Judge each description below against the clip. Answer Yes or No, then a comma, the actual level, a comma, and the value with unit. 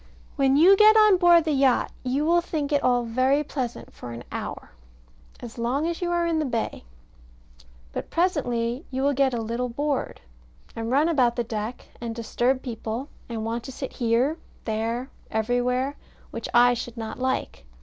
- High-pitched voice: Yes, very high, 255 Hz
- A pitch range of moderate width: Yes, average, 3.8 semitones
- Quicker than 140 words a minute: Yes, average, 180 wpm